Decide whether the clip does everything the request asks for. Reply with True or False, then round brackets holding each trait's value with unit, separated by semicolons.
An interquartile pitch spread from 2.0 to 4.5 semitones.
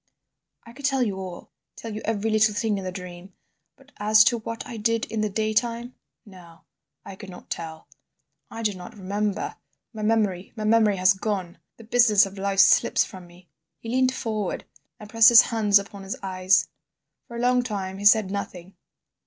True (3.0 semitones)